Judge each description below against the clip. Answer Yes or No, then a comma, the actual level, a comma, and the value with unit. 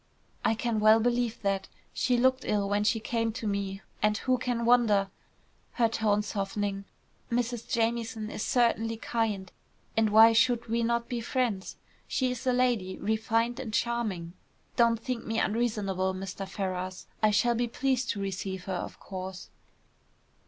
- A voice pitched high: Yes, high, 225 Hz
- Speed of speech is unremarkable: Yes, average, 160 wpm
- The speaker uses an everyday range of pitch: Yes, average, 3.0 semitones